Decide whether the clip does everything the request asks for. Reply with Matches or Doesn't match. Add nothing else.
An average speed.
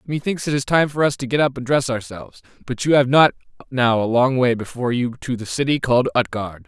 Doesn't match